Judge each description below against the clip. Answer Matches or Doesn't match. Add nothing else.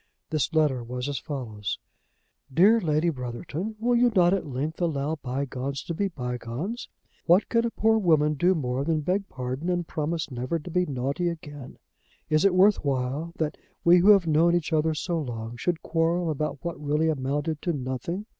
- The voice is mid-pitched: Matches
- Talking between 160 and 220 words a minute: Matches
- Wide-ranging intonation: Doesn't match